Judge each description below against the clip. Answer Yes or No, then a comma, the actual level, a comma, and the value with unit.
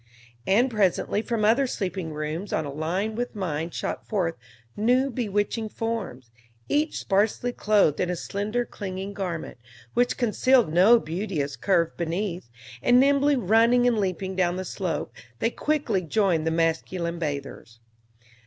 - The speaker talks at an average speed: Yes, average, 145 wpm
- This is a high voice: Yes, high, 195 Hz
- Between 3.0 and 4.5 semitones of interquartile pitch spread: No, average, 5.3 semitones